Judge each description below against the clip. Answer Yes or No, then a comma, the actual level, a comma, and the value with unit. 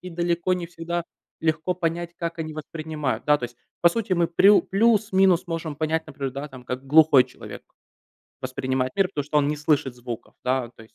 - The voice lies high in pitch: No, medium, 160 Hz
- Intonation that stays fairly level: No, average, 4.0 semitones